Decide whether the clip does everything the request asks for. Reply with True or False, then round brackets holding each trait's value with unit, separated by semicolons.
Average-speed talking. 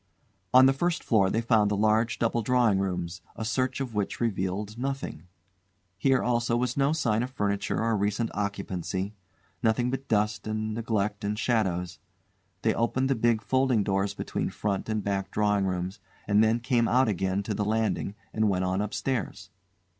True (175 wpm)